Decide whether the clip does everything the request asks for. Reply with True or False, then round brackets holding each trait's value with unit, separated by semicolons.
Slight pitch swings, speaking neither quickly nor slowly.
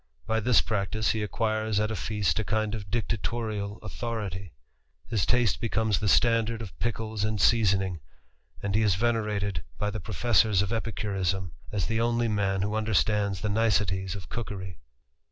True (2.3 semitones; 160 wpm)